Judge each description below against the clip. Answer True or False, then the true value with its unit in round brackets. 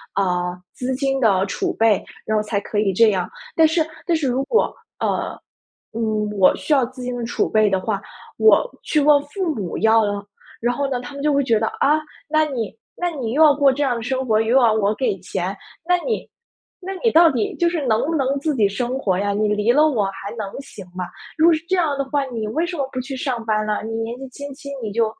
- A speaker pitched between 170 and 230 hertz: False (250 Hz)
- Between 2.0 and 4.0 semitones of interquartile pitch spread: False (5.1 semitones)